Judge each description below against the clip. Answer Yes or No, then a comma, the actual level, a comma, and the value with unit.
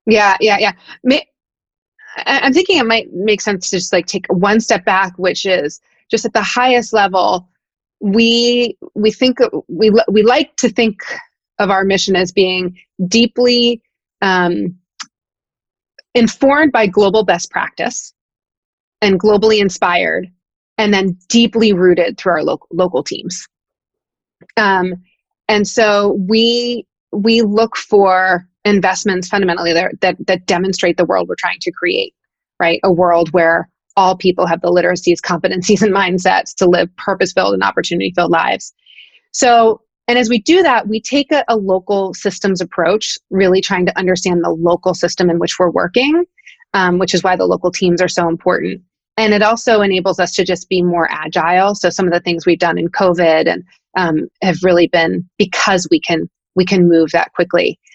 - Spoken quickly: No, average, 165 wpm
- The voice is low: No, high, 195 Hz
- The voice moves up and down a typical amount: Yes, average, 3.8 semitones